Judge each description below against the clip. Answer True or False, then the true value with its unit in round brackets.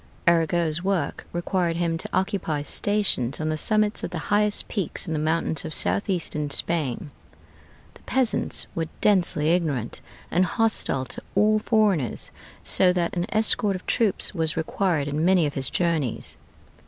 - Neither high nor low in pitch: True (170 Hz)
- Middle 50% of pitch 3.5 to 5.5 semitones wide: True (4.2 semitones)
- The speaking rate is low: False (155 wpm)